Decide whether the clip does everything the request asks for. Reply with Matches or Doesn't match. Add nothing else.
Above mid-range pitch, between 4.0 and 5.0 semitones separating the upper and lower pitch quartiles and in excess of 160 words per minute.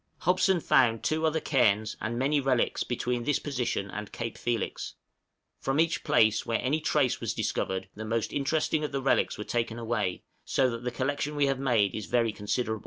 Doesn't match